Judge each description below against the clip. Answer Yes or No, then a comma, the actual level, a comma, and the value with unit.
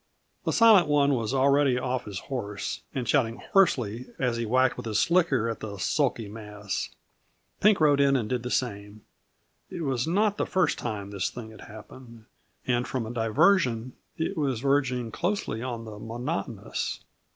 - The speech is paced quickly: No, average, 170 wpm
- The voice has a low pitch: Yes, low, 125 Hz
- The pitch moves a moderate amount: Yes, average, 4.1 semitones